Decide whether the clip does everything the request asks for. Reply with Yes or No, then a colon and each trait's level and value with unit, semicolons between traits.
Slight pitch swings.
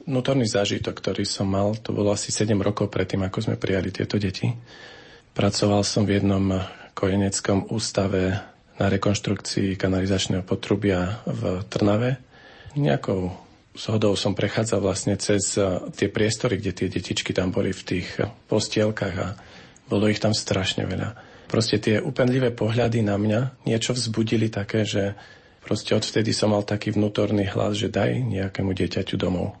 Yes: narrow, 2.2 semitones